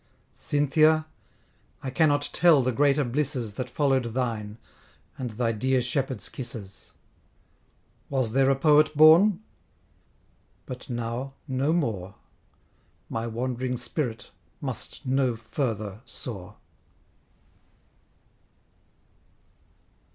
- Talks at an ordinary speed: No, slow, 90 wpm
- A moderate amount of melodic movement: Yes, average, 3.8 semitones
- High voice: No, low, 130 Hz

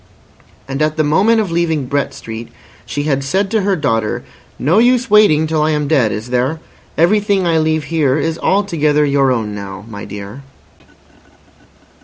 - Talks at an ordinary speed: Yes, average, 170 wpm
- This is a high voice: No, medium, 150 Hz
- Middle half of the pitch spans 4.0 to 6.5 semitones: Yes, average, 4.7 semitones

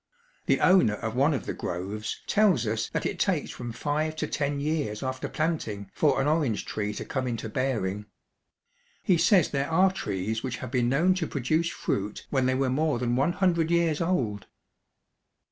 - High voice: No, low, 135 Hz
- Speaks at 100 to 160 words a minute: No, average, 185 wpm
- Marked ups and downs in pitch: Yes, wide, 6.2 semitones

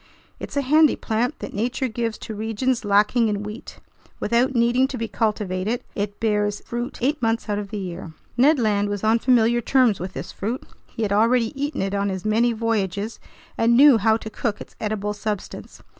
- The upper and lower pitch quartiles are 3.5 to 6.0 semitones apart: No, average, 2.7 semitones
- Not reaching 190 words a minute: No, average, 195 wpm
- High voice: Yes, high, 225 Hz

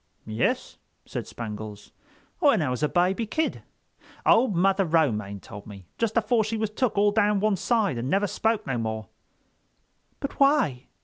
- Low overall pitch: No, high, 190 Hz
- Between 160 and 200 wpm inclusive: Yes, average, 165 wpm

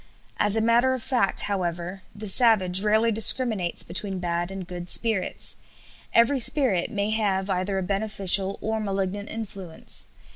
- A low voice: No, high, 200 Hz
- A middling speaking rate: Yes, average, 145 wpm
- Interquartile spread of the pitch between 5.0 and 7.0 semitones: No, average, 3.0 semitones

